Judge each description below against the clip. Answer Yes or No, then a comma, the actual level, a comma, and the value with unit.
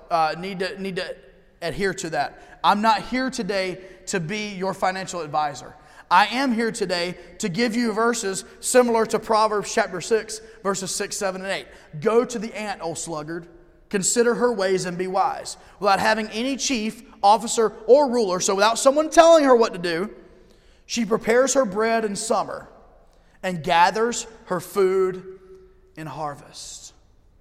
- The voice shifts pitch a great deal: No, average, 3.7 semitones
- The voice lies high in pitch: Yes, high, 200 Hz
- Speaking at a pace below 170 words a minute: Yes, average, 160 wpm